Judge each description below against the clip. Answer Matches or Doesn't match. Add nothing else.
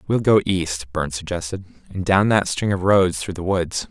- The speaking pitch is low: Matches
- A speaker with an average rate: Doesn't match